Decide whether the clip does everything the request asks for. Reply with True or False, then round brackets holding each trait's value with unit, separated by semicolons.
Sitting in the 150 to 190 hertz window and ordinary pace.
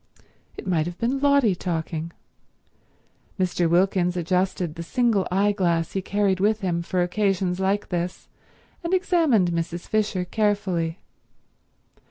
False (185 Hz; 125 wpm)